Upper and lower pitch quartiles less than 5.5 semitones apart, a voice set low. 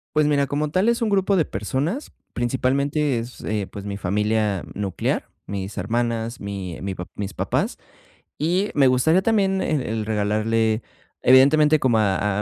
No: wide, 6.5 semitones; low, 120 Hz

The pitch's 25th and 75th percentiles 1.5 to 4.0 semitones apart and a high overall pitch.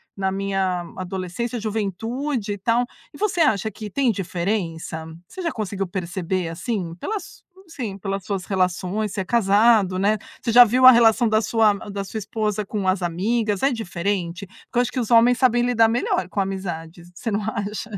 Yes: average, 3.7 semitones; high, 205 Hz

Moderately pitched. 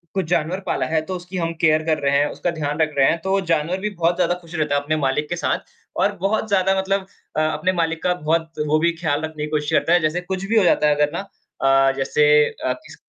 Yes: medium, 165 Hz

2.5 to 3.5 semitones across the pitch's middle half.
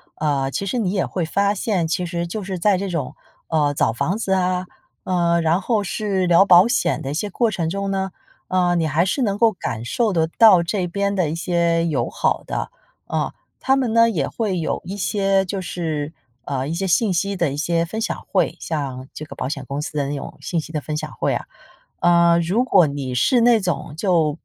No: average, 4.0 semitones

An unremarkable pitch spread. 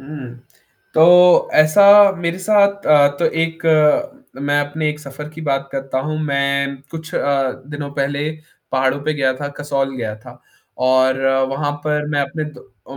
No: narrow, 2.2 semitones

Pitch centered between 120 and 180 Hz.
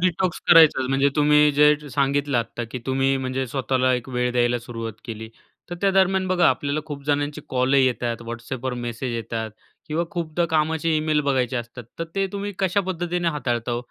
Yes: medium, 140 Hz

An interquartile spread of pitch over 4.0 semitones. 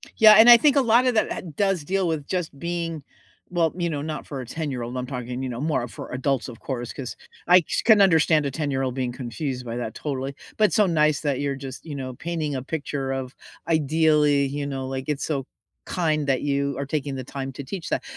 No: average, 3.7 semitones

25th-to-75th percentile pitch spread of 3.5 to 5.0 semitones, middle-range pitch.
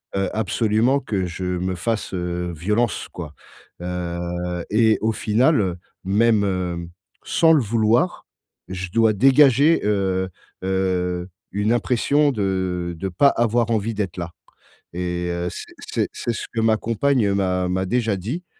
No: average, 4.3 semitones; low, 100 Hz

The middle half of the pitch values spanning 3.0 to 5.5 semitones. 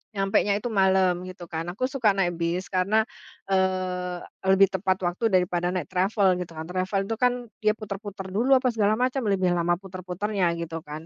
No: narrow, 2.6 semitones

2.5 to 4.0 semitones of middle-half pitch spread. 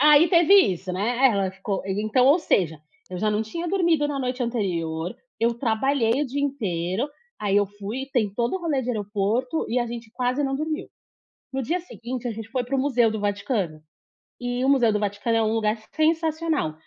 No: average, 5.2 semitones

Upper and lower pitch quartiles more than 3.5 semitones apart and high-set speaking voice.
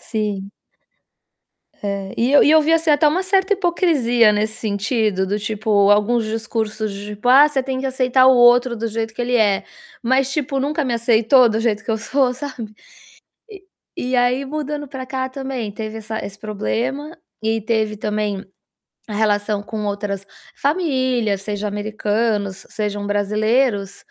Yes: average, 4.0 semitones; high, 225 Hz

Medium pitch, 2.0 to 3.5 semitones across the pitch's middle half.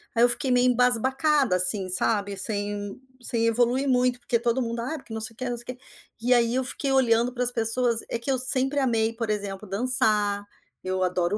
No: high, 235 Hz; average, 3.1 semitones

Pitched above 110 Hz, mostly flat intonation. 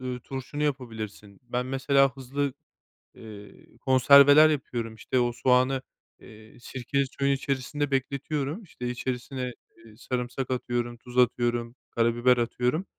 Yes: low, 125 Hz; narrow, 2.3 semitones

